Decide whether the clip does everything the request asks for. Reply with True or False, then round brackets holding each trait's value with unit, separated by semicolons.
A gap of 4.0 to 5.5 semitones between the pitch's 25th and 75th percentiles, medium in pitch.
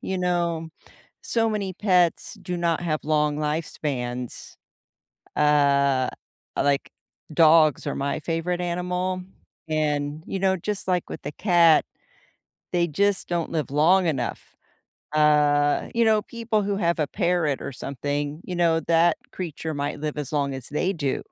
False (3.6 semitones; 160 Hz)